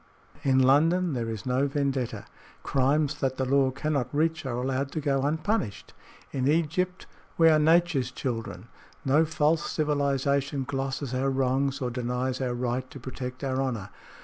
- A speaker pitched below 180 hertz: Yes, low, 135 Hz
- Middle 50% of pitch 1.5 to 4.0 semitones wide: Yes, narrow, 2.6 semitones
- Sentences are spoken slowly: No, average, 155 wpm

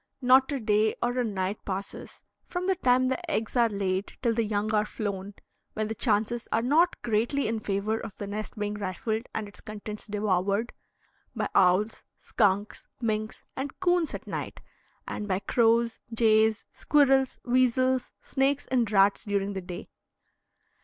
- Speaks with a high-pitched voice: Yes, high, 220 Hz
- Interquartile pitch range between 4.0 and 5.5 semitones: No, average, 3.4 semitones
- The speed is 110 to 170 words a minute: Yes, average, 160 wpm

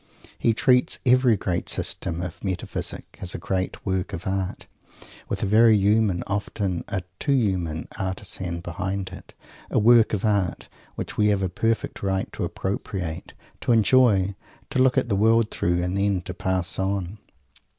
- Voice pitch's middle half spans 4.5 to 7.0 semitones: No, average, 3.1 semitones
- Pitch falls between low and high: No, very low, 95 Hz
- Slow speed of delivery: No, average, 165 wpm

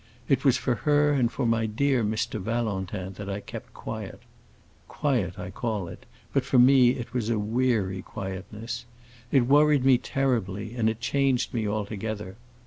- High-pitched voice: No, low, 115 Hz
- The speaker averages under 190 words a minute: Yes, average, 160 wpm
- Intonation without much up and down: No, average, 3.8 semitones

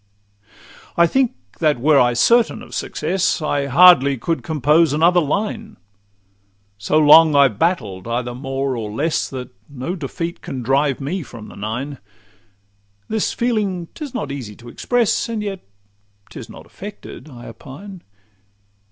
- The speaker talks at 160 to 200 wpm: No, average, 145 wpm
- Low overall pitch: No, medium, 150 Hz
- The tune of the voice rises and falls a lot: Yes, wide, 5.9 semitones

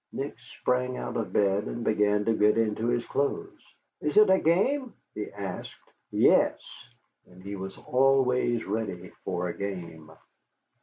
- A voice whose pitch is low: Yes, low, 110 Hz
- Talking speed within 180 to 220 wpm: No, average, 145 wpm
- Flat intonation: No, average, 4.3 semitones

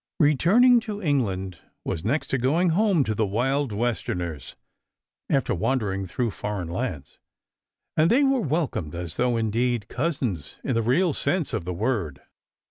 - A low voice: Yes, low, 120 Hz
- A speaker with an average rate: Yes, average, 155 wpm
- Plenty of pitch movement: Yes, wide, 8.2 semitones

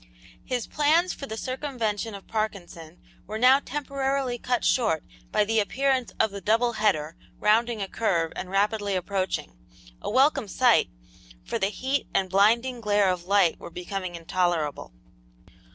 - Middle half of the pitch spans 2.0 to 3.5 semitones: No, average, 5.0 semitones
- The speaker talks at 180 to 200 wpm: No, average, 150 wpm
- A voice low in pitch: No, high, 215 Hz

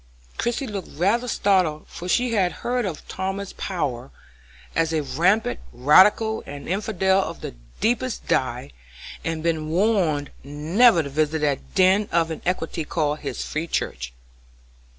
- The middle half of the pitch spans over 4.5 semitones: Yes, average, 5.0 semitones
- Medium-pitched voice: Yes, medium, 170 Hz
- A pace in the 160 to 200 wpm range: No, average, 140 wpm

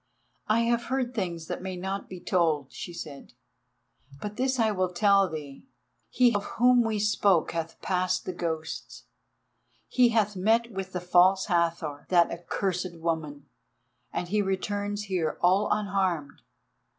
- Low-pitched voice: No, medium, 185 Hz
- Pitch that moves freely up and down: No, average, 3.6 semitones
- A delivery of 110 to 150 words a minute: Yes, average, 140 wpm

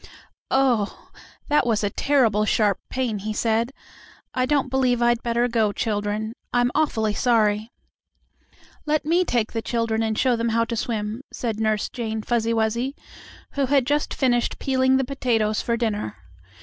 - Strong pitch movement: No, average, 2.8 semitones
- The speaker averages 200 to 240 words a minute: No, average, 160 wpm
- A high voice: Yes, high, 235 Hz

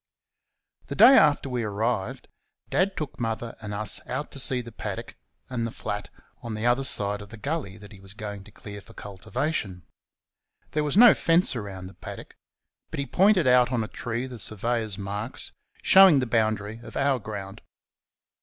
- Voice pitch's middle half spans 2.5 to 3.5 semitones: No, average, 4.6 semitones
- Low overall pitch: Yes, low, 115 Hz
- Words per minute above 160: Yes, average, 180 wpm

